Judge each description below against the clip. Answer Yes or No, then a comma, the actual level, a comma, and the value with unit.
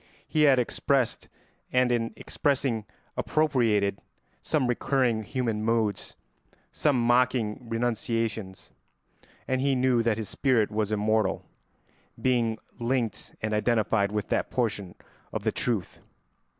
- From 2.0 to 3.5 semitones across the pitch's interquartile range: Yes, average, 2.8 semitones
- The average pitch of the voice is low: Yes, low, 115 Hz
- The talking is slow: Yes, slow, 115 wpm